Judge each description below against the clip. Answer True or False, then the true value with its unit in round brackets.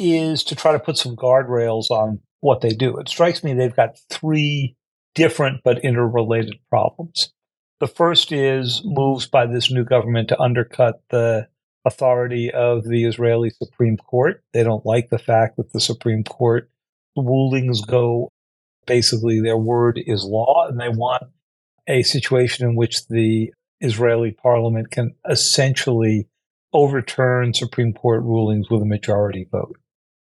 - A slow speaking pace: False (145 wpm)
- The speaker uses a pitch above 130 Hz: False (120 Hz)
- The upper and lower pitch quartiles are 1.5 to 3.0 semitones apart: True (2.6 semitones)